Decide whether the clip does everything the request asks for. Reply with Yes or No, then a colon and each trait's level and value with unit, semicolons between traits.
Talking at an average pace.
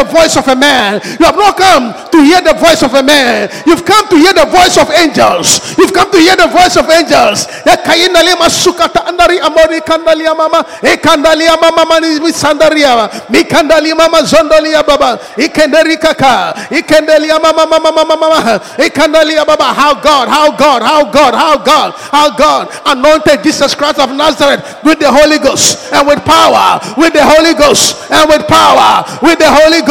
Yes: average, 145 wpm